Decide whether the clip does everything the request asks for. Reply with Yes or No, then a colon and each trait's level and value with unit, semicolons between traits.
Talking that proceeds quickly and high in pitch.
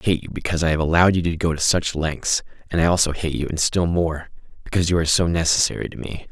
No: fast, 255 wpm; very low, 85 Hz